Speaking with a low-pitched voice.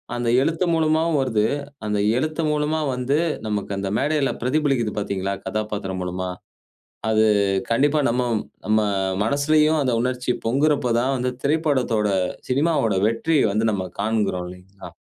Yes: low, 125 Hz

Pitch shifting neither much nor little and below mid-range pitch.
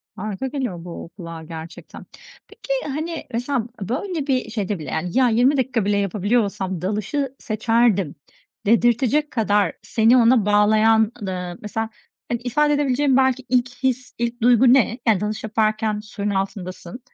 No: average, 3.9 semitones; high, 225 Hz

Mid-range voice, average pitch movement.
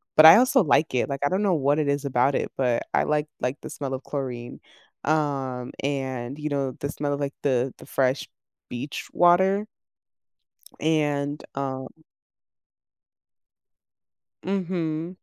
Yes: medium, 145 Hz; average, 3.0 semitones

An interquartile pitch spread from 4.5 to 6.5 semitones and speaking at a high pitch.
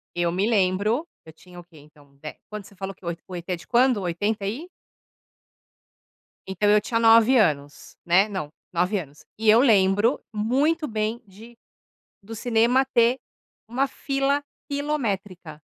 Yes: average, 4.9 semitones; high, 210 Hz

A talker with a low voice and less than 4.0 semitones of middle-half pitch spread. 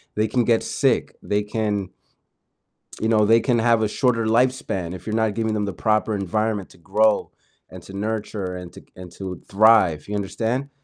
Yes: low, 110 Hz; narrow, 2.5 semitones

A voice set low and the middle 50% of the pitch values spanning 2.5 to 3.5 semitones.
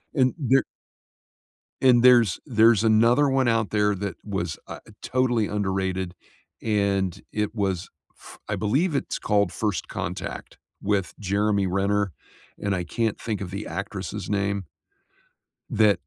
Yes: low, 105 Hz; average, 2.9 semitones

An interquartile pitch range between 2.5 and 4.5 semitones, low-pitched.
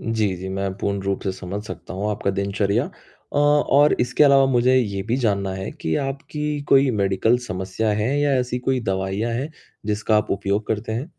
No: average, 4.9 semitones; low, 110 Hz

